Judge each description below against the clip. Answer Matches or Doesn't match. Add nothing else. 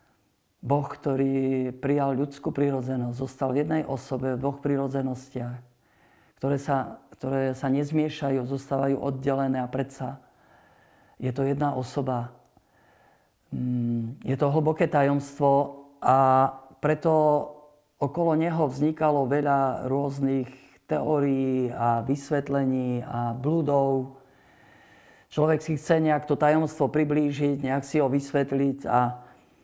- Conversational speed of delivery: Doesn't match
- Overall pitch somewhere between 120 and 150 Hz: Matches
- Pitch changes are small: Matches